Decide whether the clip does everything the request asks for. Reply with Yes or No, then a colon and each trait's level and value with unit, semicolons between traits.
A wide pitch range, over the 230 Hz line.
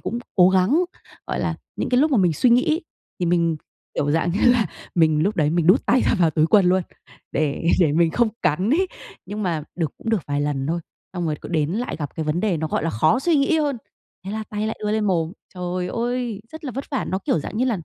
No: wide, 6.5 semitones; medium, 185 Hz